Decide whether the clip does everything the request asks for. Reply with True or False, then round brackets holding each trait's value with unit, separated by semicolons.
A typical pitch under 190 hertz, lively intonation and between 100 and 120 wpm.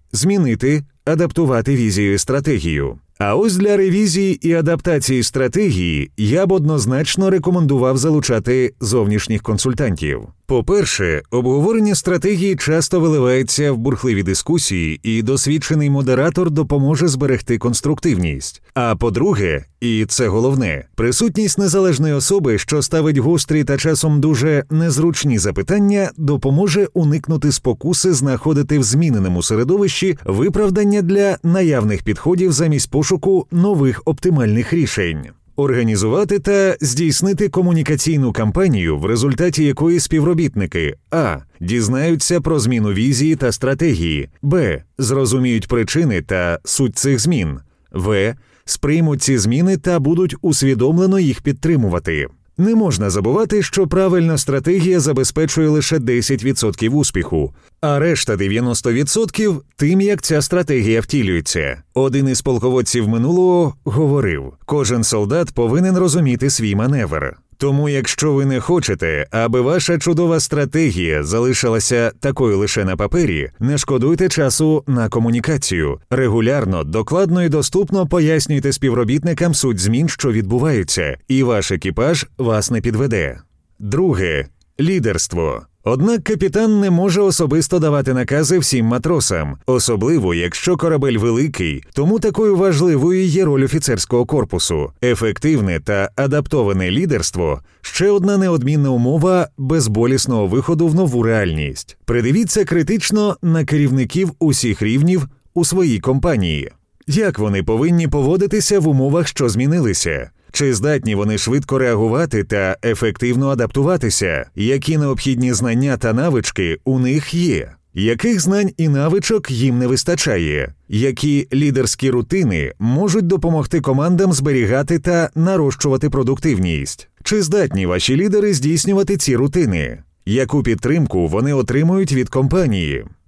True (140 Hz; 6.5 semitones; 115 wpm)